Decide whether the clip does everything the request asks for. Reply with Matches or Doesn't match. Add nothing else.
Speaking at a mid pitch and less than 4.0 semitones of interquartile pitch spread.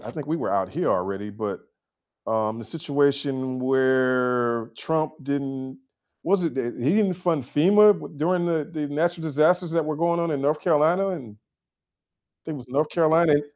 Doesn't match